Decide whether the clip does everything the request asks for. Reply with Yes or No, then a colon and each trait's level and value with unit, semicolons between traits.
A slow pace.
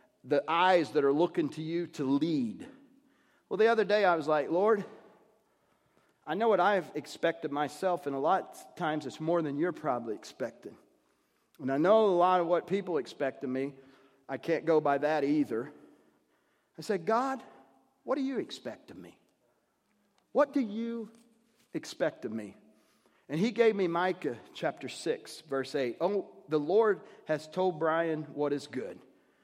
No: average, 170 wpm